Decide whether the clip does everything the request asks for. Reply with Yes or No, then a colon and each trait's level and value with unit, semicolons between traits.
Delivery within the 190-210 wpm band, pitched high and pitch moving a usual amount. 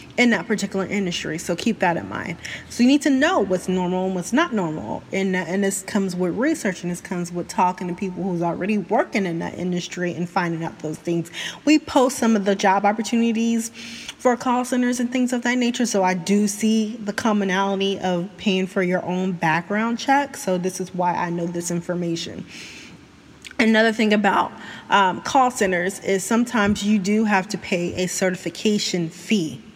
Yes: average, 195 wpm; high, 195 Hz; average, 4.0 semitones